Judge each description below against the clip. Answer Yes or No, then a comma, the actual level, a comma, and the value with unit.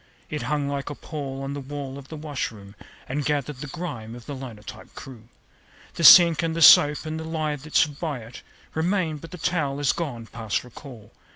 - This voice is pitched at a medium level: Yes, medium, 145 Hz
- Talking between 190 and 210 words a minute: Yes, fast, 205 wpm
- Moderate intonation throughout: Yes, average, 3.5 semitones